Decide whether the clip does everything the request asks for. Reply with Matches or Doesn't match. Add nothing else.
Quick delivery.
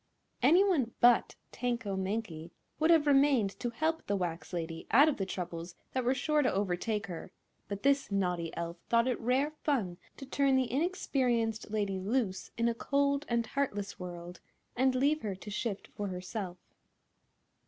Doesn't match